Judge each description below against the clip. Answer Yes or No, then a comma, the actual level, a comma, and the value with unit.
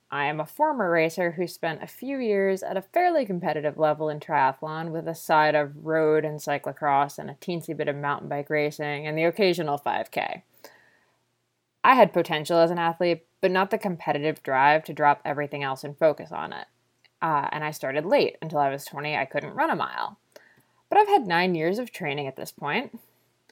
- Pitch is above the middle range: No, medium, 155 Hz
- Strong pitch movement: No, average, 3.3 semitones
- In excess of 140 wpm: Yes, average, 200 wpm